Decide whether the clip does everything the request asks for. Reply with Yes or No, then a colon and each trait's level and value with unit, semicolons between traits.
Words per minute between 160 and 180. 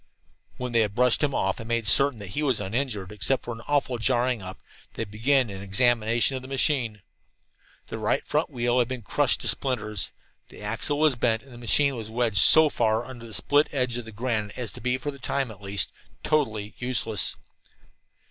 No: fast, 205 wpm